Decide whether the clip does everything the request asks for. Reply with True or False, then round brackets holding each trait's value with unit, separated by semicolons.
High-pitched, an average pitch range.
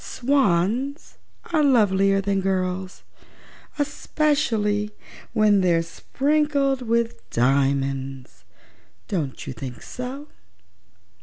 False (205 Hz; 8.0 semitones)